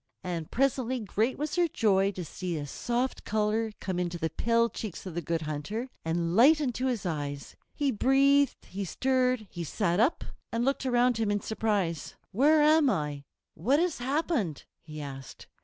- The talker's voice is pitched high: Yes, high, 220 Hz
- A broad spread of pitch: Yes, wide, 7.2 semitones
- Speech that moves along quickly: No, average, 175 wpm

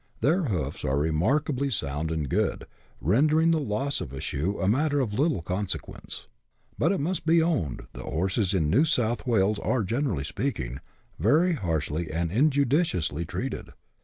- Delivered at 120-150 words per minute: No, average, 160 wpm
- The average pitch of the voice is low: Yes, low, 105 Hz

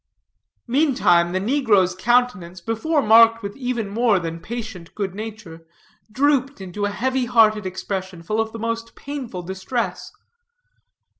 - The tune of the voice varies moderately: Yes, average, 4.4 semitones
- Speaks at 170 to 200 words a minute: No, slow, 135 wpm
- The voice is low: No, high, 220 Hz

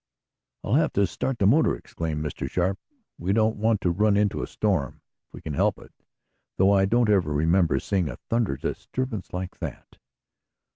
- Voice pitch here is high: No, very low, 95 Hz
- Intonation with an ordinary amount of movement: Yes, average, 4.1 semitones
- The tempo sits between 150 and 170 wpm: No, average, 185 wpm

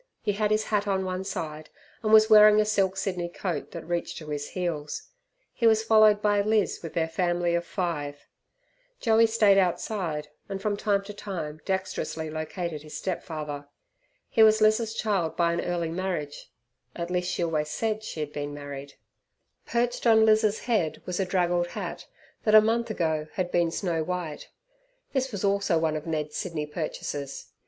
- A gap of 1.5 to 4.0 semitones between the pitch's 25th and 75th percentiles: No, average, 5.0 semitones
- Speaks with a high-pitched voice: No, medium, 180 Hz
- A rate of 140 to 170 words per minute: No, average, 180 wpm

